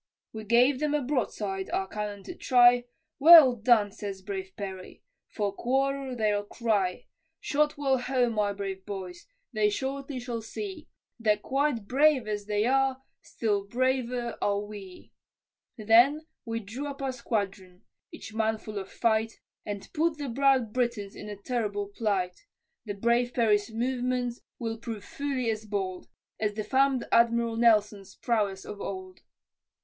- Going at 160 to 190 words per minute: No, average, 150 wpm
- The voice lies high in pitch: Yes, high, 225 Hz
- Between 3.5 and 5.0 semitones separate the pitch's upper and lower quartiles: Yes, average, 3.9 semitones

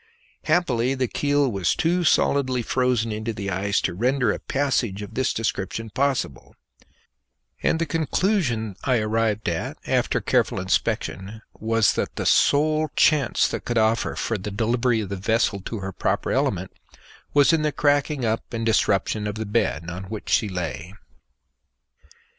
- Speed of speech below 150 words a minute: No, average, 160 wpm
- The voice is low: Yes, low, 115 Hz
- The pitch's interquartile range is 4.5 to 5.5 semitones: Yes, average, 4.8 semitones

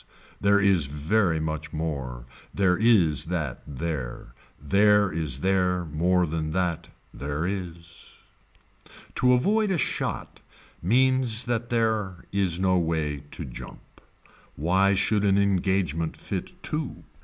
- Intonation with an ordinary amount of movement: Yes, average, 4.5 semitones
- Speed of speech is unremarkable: No, slow, 120 wpm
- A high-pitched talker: No, very low, 90 Hz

